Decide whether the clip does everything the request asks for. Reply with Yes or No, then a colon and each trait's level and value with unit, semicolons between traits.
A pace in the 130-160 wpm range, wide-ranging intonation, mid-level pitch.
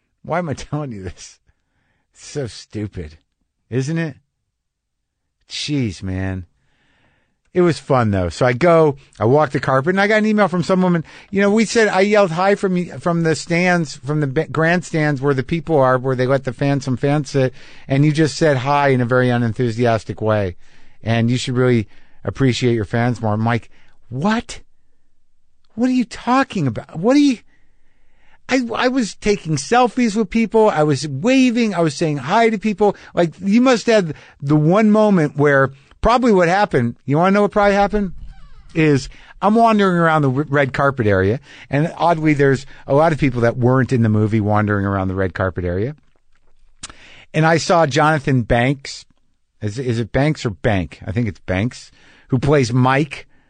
No: average, 185 wpm; wide, 7.0 semitones; medium, 145 Hz